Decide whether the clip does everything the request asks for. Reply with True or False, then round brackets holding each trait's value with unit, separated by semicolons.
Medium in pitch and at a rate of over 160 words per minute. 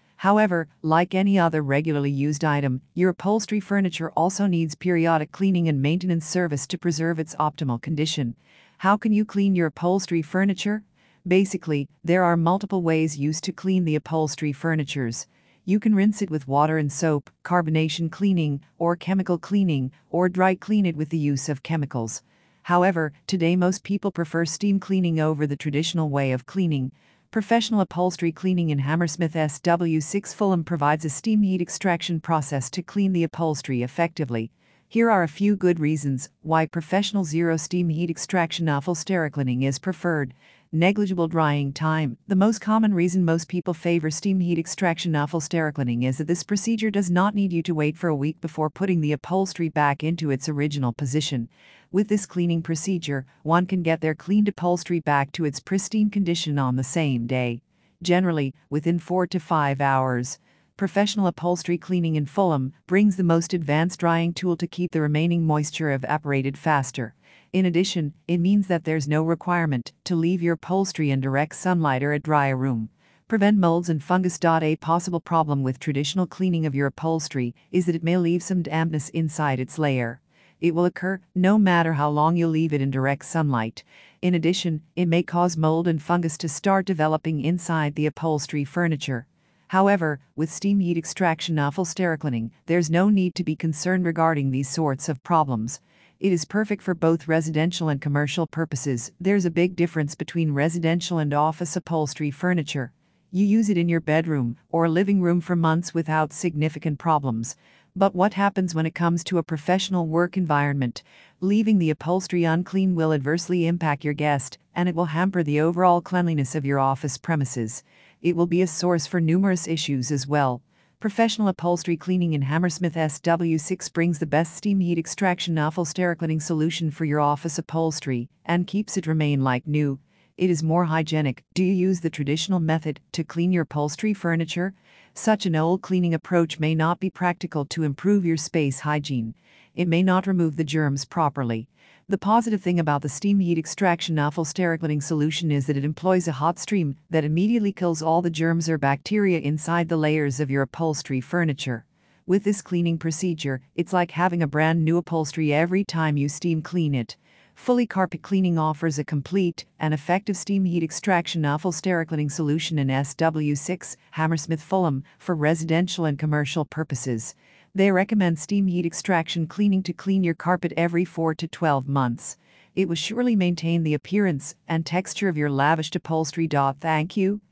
True (165 Hz; 175 wpm)